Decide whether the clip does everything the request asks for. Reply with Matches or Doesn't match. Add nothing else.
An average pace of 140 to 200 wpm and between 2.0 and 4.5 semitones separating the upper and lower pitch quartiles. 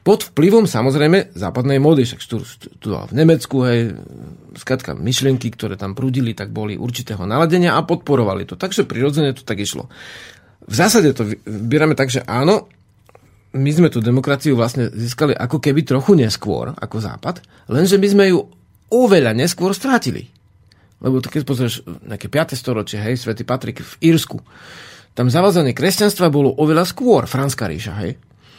Doesn't match